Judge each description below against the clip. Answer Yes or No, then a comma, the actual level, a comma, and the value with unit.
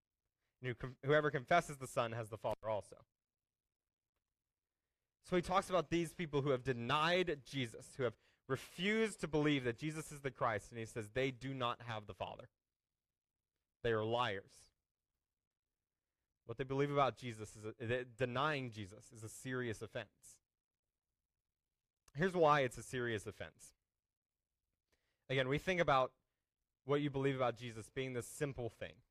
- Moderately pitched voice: No, low, 130 Hz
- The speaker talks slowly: No, average, 155 wpm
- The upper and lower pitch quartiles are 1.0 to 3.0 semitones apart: No, average, 4.0 semitones